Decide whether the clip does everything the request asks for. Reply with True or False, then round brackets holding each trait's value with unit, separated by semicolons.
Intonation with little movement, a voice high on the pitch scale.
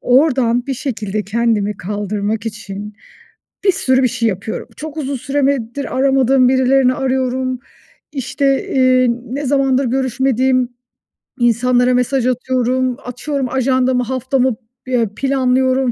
True (2.0 semitones; 255 Hz)